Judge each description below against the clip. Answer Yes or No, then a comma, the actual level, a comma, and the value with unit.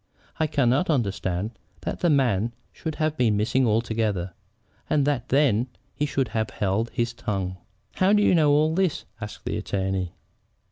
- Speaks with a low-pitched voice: Yes, low, 120 Hz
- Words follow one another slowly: No, average, 160 wpm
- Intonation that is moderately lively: No, wide, 6.1 semitones